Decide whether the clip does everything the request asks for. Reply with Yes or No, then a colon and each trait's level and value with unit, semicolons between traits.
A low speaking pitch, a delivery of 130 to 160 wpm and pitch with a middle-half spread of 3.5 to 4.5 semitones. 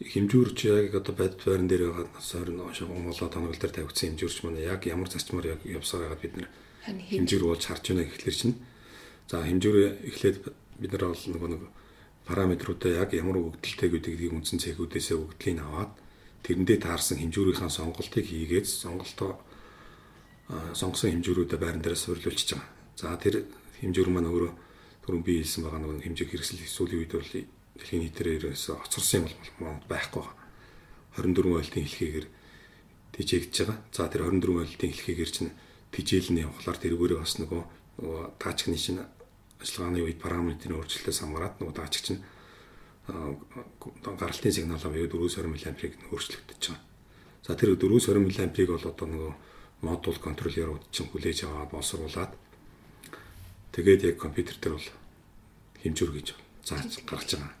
No: very low, 85 Hz; average, 140 wpm; average, 2.8 semitones